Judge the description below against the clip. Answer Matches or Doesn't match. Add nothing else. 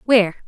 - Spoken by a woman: Matches